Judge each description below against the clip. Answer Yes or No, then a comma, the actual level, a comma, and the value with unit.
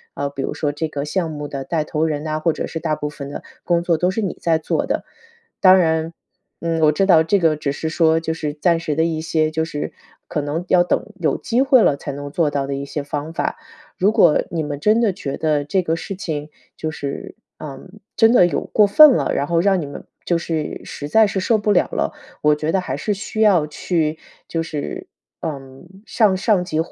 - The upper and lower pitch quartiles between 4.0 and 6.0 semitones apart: No, average, 3.5 semitones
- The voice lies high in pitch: No, medium, 160 Hz